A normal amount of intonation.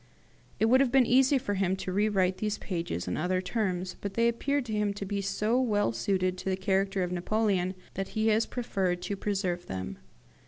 Yes: average, 3.0 semitones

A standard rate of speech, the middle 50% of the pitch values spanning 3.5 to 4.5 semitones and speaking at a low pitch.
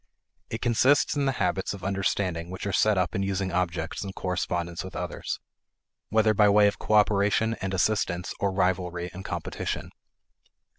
No: average, 160 wpm; narrow, 2.5 semitones; very low, 95 Hz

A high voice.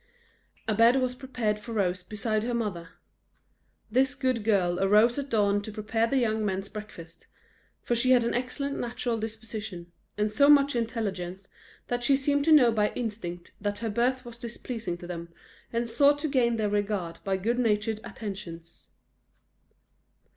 Yes: high, 225 Hz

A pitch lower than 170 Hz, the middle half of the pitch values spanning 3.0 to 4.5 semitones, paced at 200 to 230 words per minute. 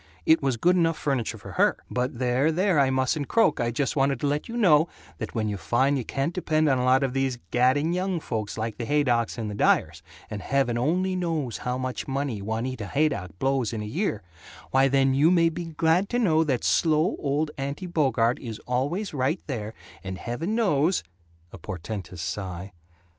No: low, 135 Hz; average, 5.1 semitones; fast, 205 wpm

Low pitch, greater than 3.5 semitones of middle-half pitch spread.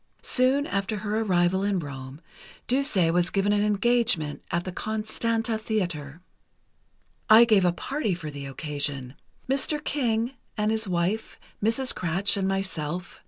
No: high, 200 Hz; average, 4.6 semitones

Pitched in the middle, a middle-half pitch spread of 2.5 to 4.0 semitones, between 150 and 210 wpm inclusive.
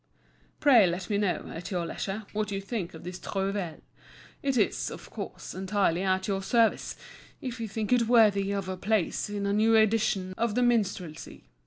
No: high, 200 Hz; average, 2.9 semitones; average, 185 wpm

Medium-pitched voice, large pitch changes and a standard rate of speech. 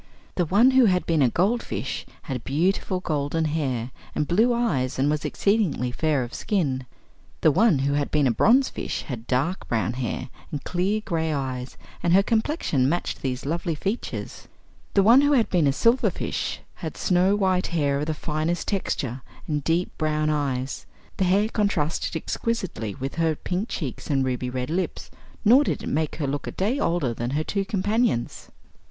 Yes: medium, 160 Hz; wide, 6.2 semitones; average, 180 wpm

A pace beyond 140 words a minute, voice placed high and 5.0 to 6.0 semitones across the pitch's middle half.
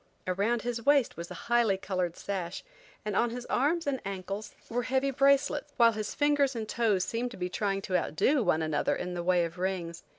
Yes: fast, 205 wpm; high, 215 Hz; average, 5.3 semitones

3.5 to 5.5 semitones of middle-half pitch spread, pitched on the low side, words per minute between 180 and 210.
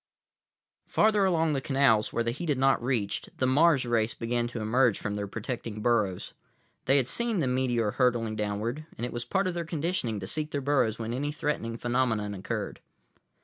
Yes: average, 4.6 semitones; low, 125 Hz; average, 195 wpm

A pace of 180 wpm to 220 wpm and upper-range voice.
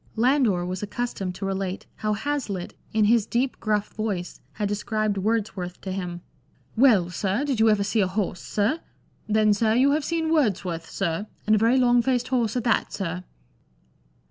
Yes: average, 190 wpm; high, 215 Hz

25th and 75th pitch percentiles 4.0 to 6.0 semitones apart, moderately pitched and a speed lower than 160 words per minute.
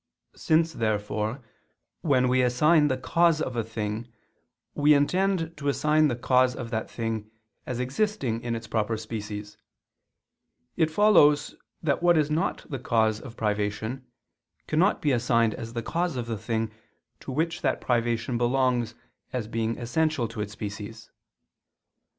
No: average, 5.2 semitones; low, 120 Hz; average, 150 wpm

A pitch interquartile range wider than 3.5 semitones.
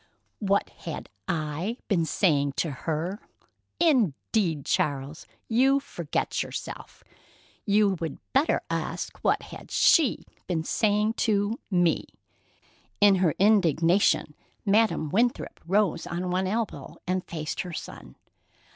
Yes: average, 4.8 semitones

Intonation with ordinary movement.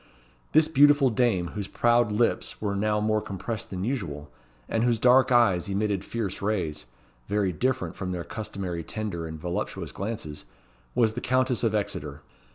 Yes: average, 4.3 semitones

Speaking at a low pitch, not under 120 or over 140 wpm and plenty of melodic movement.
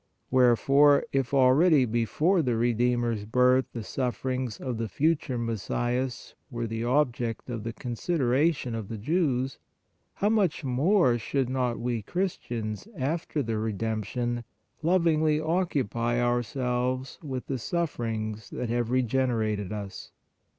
No: low, 125 Hz; slow, 135 wpm; average, 3.3 semitones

